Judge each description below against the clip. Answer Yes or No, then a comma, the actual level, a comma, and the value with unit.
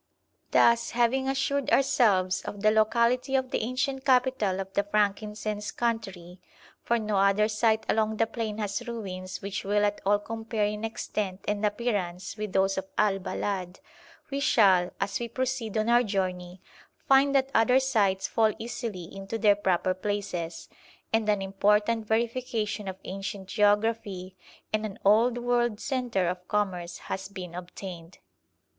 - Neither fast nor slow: Yes, average, 150 wpm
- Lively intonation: No, average, 3.3 semitones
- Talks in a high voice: Yes, high, 210 Hz